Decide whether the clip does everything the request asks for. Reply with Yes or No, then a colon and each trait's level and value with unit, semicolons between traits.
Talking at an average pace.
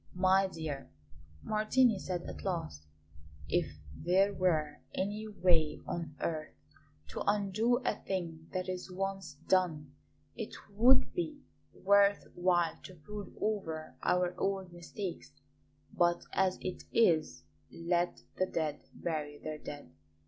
No: slow, 125 wpm